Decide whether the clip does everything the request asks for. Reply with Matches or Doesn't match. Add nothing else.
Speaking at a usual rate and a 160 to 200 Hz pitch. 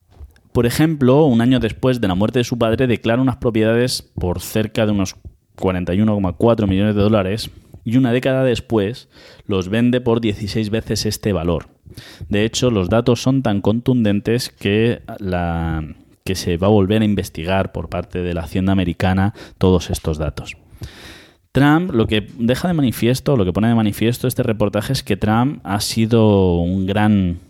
Doesn't match